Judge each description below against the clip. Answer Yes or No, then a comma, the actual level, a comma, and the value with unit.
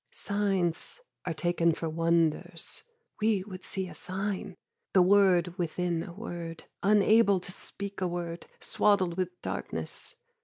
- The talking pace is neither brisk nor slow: No, slow, 130 wpm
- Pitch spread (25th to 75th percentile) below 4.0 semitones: Yes, average, 2.7 semitones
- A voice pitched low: No, medium, 180 Hz